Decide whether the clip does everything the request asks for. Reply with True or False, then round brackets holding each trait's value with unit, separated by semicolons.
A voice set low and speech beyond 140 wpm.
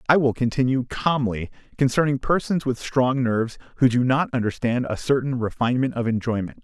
True (125 Hz; 165 wpm)